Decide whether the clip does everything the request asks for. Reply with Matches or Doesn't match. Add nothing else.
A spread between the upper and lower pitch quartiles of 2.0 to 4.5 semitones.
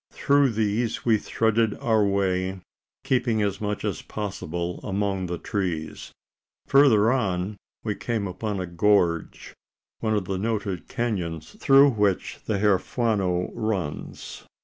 Matches